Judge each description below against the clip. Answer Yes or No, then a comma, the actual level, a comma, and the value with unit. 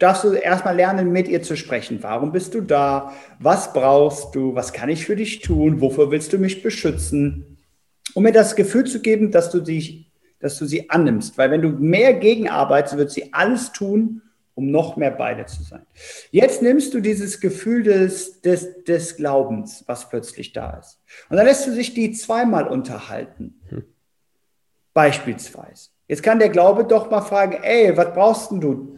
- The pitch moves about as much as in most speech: No, wide, 7.1 semitones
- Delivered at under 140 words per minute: No, average, 175 wpm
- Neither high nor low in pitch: Yes, medium, 180 Hz